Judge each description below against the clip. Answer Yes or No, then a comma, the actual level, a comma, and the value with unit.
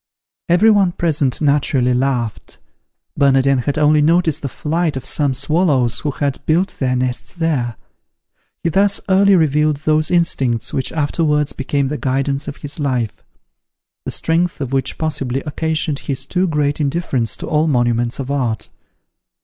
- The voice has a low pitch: No, medium, 145 Hz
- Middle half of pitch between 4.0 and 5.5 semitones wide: No, average, 3.4 semitones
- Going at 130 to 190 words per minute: Yes, average, 150 wpm